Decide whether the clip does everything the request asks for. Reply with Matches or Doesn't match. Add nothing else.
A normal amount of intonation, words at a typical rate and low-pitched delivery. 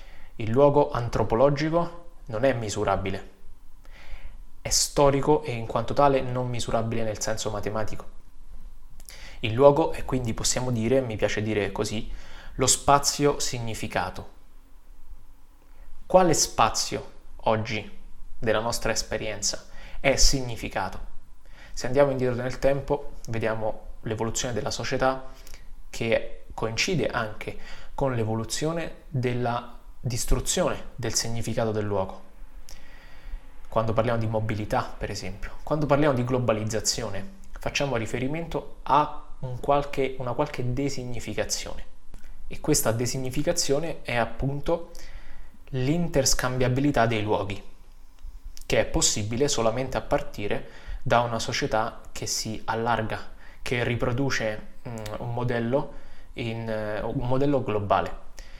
Doesn't match